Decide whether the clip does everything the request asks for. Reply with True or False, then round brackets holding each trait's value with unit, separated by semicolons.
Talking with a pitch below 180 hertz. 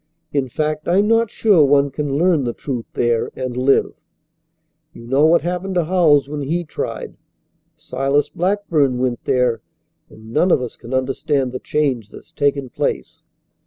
True (140 Hz)